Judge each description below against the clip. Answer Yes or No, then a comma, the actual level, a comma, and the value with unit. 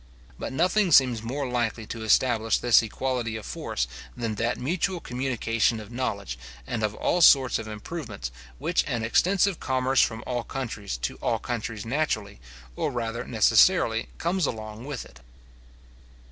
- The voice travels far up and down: No, average, 3.4 semitones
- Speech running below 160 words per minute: Yes, average, 150 wpm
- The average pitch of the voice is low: Yes, low, 120 Hz